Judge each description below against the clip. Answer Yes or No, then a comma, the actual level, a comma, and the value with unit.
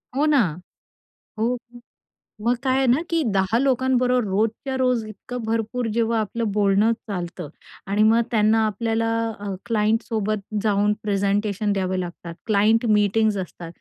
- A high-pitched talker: Yes, high, 220 Hz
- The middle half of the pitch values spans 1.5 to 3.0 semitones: Yes, average, 2.7 semitones